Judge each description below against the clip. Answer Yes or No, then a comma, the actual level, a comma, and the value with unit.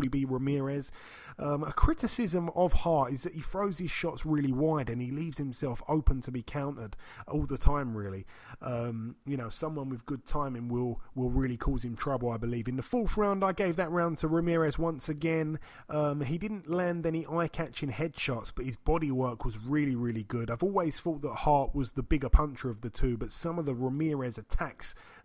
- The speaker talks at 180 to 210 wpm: Yes, fast, 205 wpm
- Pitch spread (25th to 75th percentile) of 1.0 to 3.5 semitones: No, average, 4.6 semitones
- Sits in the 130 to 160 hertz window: Yes, medium, 140 Hz